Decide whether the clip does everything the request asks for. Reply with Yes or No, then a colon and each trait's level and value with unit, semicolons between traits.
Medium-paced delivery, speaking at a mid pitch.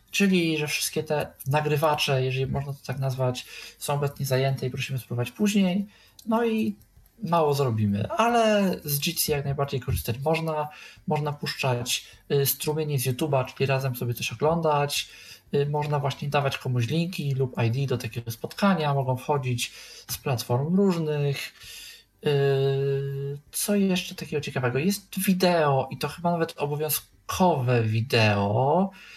Yes: average, 140 wpm; medium, 145 Hz